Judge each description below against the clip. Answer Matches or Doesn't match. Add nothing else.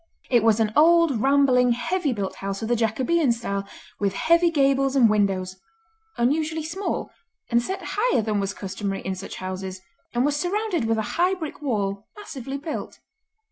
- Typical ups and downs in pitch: Doesn't match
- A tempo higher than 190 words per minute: Doesn't match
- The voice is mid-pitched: Doesn't match